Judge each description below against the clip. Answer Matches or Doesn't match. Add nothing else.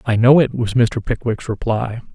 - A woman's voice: Doesn't match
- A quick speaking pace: Doesn't match